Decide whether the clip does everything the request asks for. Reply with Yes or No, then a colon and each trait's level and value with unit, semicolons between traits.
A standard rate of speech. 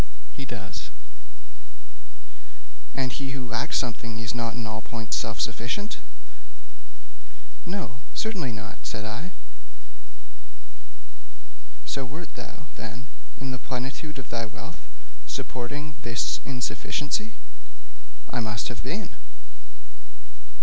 No: slow, 105 wpm